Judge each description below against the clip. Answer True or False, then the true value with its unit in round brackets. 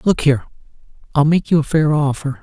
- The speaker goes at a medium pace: True (175 wpm)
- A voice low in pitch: False (150 Hz)